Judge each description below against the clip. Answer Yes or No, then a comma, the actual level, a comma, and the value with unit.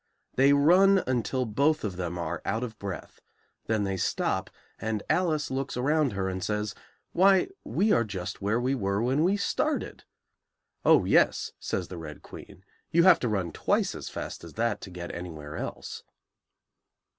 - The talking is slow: No, average, 170 wpm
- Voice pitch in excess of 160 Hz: No, low, 110 Hz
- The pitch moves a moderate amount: No, wide, 7.2 semitones